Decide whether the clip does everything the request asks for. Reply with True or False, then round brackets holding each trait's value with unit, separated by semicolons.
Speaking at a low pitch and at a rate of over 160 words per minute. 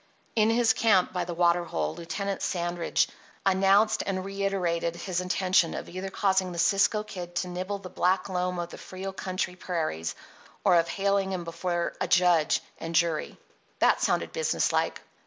False (185 Hz; 170 wpm)